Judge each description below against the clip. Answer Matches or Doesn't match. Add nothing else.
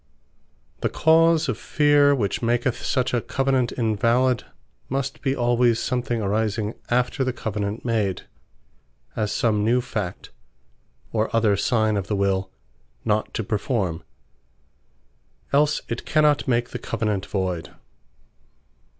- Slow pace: Matches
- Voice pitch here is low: Matches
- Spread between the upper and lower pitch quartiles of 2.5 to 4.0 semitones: Matches